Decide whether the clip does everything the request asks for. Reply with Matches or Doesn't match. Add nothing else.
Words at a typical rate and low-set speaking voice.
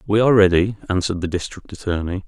Matches